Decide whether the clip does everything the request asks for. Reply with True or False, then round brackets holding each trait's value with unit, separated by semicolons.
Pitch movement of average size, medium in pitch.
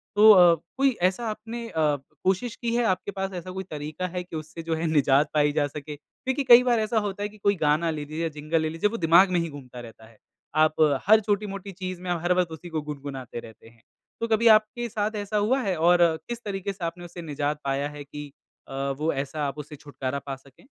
False (5.7 semitones; 170 Hz)